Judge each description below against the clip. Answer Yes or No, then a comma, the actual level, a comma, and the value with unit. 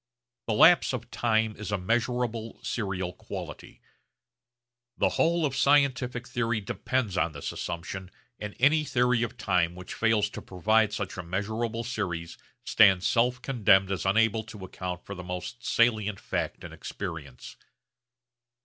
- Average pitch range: Yes, average, 4.4 semitones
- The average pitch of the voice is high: No, low, 110 Hz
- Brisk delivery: No, average, 145 wpm